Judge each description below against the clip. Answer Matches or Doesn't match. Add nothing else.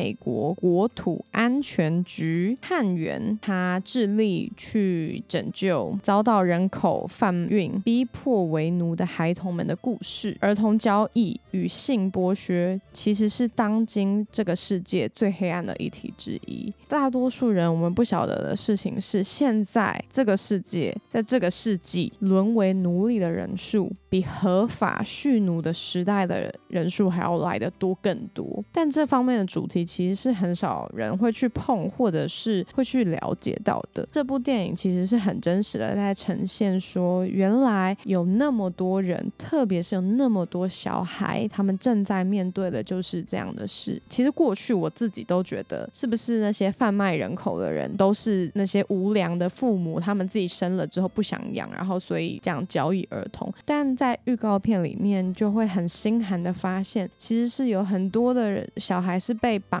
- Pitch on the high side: Matches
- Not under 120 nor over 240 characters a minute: Doesn't match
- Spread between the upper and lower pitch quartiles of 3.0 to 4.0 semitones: Matches